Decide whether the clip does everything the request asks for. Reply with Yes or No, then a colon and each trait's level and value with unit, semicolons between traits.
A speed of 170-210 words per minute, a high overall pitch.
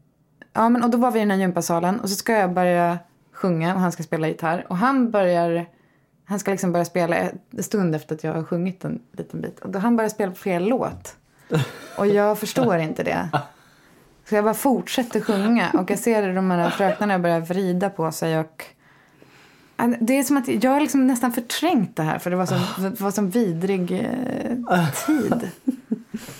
Yes: fast, 195 wpm; high, 195 Hz